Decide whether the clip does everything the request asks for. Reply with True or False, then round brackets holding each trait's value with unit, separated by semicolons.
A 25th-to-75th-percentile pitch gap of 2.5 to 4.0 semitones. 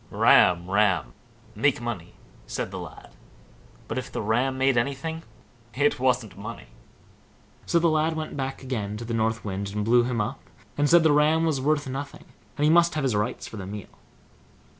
False (5.5 semitones)